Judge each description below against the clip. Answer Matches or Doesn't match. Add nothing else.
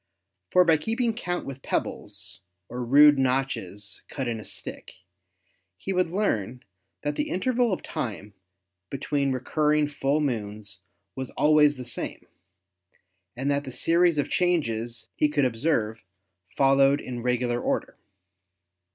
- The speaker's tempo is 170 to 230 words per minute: Doesn't match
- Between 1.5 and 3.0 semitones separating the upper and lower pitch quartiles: Doesn't match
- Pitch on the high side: Doesn't match